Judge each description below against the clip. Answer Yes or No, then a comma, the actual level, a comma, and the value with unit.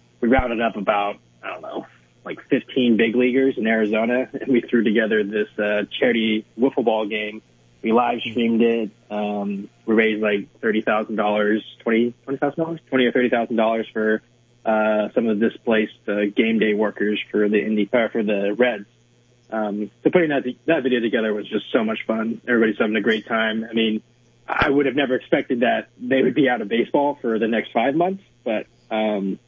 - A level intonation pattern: Yes, narrow, 2.3 semitones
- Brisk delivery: No, average, 190 wpm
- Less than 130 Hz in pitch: Yes, low, 110 Hz